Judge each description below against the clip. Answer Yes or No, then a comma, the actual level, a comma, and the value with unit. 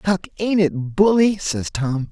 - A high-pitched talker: No, medium, 170 Hz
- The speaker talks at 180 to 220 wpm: No, average, 170 wpm